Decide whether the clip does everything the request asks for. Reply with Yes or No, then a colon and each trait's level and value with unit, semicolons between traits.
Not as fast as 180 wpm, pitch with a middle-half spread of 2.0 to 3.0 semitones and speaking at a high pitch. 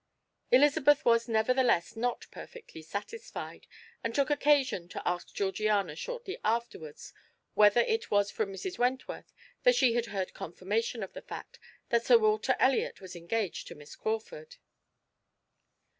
No: average, 140 wpm; wide, 5.4 semitones; high, 230 Hz